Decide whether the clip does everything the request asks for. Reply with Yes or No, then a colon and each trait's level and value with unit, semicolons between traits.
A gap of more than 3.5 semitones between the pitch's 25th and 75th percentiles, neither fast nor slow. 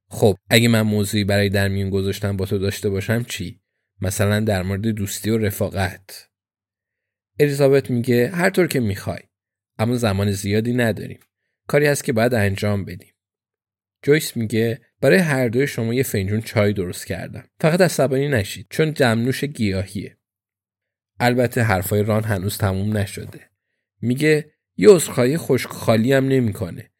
Yes: average, 3.9 semitones; average, 140 wpm